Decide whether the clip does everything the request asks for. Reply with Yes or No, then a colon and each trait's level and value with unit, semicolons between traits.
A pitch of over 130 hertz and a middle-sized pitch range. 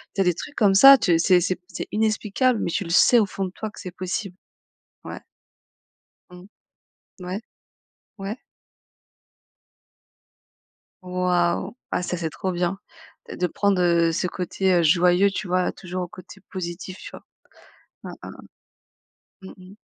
No: medium, 185 Hz; narrow, 1.8 semitones